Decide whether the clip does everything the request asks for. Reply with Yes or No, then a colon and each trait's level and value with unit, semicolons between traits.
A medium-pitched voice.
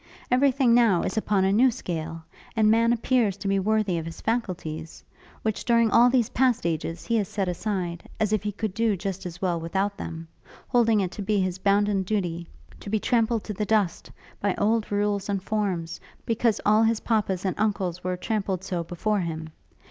No: high, 205 Hz